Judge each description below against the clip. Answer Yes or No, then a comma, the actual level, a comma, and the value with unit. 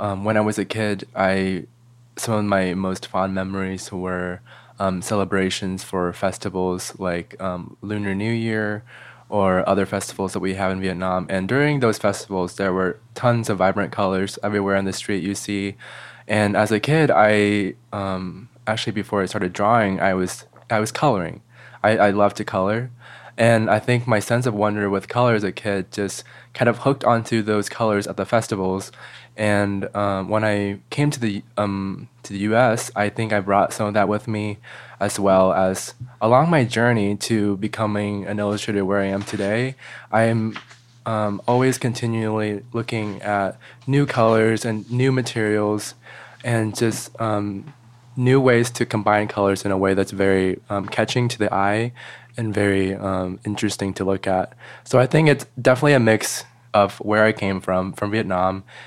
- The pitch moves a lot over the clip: No, average, 2.9 semitones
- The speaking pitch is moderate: No, low, 105 Hz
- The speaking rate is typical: Yes, average, 175 wpm